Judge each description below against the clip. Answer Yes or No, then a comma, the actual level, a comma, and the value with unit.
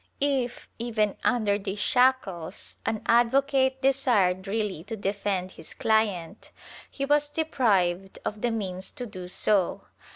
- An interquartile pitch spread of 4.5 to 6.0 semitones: Yes, average, 5.1 semitones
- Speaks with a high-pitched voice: Yes, high, 215 Hz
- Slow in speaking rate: Yes, slow, 130 wpm